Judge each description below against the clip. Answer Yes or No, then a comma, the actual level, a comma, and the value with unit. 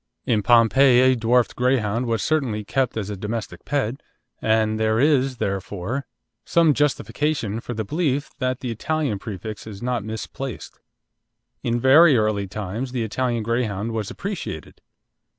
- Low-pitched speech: Yes, low, 115 Hz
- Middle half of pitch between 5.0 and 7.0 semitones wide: No, average, 3.6 semitones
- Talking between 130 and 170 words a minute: Yes, average, 145 wpm